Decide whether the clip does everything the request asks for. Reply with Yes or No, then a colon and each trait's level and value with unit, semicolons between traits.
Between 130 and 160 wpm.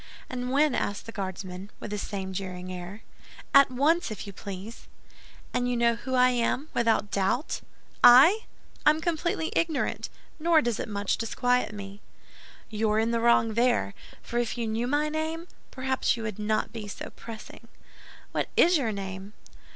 No: average, 170 wpm